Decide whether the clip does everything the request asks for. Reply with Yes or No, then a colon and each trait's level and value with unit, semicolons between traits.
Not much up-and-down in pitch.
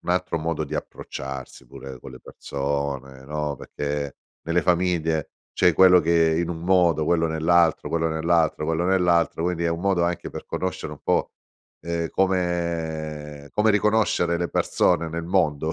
Yes: narrow, 2.3 semitones